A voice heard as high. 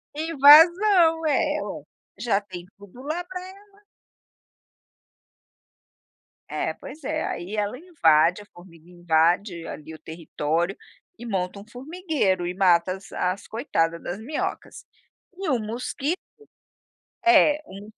Yes: high, 210 Hz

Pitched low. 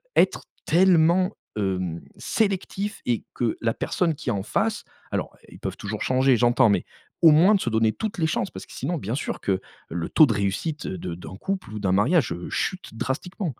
Yes: low, 130 Hz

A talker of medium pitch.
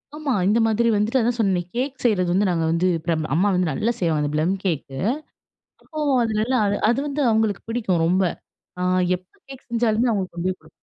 No: high, 205 Hz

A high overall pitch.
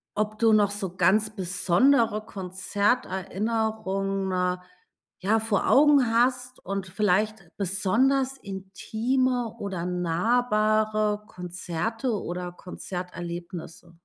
Yes: high, 205 Hz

